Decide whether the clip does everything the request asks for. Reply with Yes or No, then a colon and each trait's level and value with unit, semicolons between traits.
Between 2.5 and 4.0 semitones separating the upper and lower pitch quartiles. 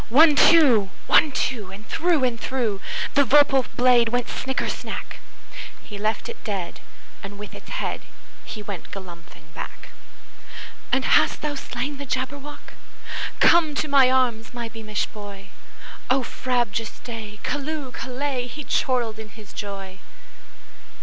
No: average, 4.5 semitones